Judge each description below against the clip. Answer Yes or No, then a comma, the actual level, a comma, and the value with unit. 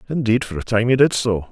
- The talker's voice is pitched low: Yes, low, 115 Hz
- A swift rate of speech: Yes, fast, 280 wpm